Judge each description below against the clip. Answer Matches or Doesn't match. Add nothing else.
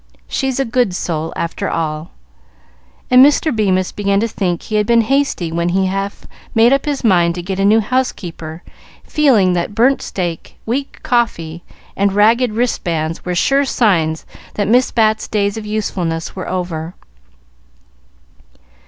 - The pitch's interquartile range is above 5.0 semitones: Matches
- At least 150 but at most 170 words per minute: Matches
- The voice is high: Matches